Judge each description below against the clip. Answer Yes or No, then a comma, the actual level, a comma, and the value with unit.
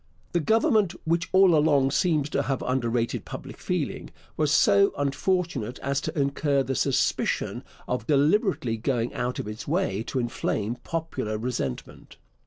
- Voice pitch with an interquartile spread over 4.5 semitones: Yes, average, 5.1 semitones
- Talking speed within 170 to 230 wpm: No, average, 145 wpm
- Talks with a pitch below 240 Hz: Yes, medium, 140 Hz